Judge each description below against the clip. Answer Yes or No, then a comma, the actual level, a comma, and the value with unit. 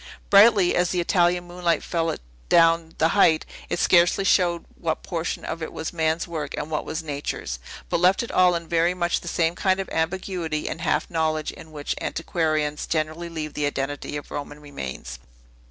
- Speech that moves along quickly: No, average, 185 wpm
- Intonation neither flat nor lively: No, narrow, 2.3 semitones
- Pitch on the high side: No, medium, 165 Hz